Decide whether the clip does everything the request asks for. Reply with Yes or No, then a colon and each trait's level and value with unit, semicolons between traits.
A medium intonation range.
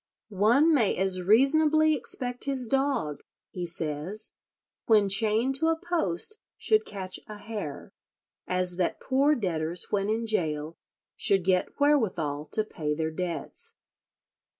No: wide, 7.4 semitones